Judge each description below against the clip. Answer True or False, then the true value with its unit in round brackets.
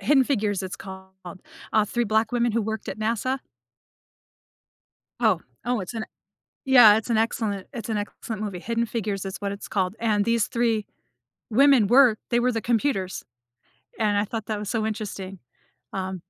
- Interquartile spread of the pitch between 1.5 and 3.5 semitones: True (2.6 semitones)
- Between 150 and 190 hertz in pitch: False (215 Hz)